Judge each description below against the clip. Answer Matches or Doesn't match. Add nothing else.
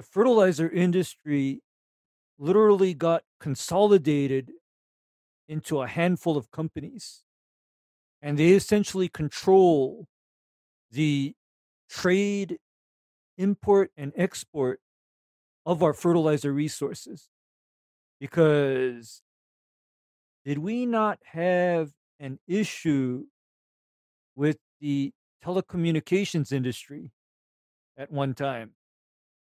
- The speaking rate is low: Matches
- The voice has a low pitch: Doesn't match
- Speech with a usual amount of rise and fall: Matches